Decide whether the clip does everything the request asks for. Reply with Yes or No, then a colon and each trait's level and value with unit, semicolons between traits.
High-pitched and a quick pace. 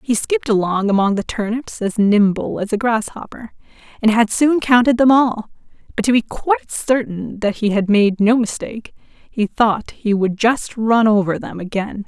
No: high, 220 Hz; average, 185 wpm